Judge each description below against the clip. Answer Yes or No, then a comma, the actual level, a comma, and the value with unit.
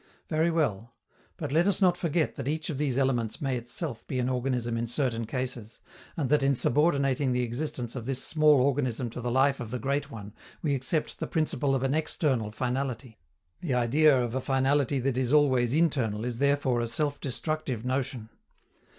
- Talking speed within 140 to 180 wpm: No, average, 190 wpm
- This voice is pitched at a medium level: No, low, 130 Hz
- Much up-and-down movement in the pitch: No, average, 3.2 semitones